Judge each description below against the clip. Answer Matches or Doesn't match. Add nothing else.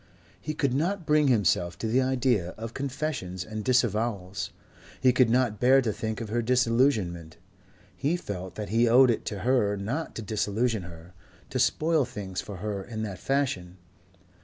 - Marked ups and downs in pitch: Doesn't match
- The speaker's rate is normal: Matches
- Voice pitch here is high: Doesn't match